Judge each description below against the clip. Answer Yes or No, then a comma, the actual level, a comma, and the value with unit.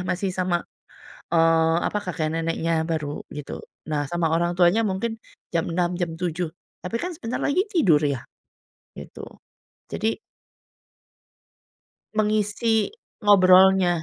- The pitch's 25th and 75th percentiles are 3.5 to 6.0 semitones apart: Yes, average, 4.0 semitones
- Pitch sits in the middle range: Yes, medium, 180 Hz